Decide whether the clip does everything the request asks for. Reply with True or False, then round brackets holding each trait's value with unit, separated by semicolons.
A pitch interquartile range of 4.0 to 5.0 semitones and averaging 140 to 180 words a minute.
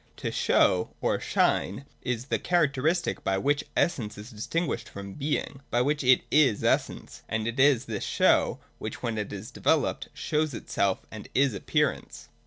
False (5.4 semitones; 170 wpm)